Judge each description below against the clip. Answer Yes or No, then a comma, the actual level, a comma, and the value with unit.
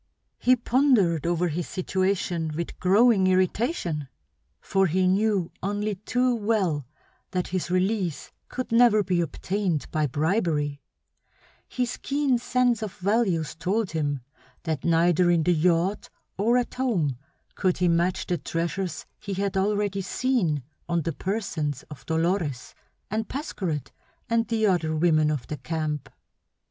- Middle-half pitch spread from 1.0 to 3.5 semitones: No, average, 4.6 semitones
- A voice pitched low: No, medium, 185 Hz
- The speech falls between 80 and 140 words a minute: Yes, slow, 135 wpm